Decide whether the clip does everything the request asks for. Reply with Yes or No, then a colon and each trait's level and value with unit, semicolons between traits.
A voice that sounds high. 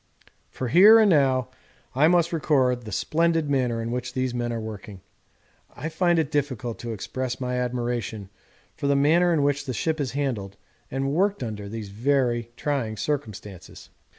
No: low, 130 Hz